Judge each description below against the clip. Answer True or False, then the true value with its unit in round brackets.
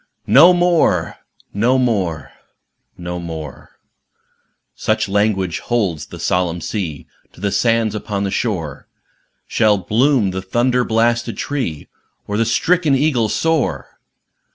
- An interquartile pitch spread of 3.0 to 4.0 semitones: False (5.3 semitones)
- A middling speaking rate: False (110 wpm)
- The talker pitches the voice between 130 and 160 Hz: False (110 Hz)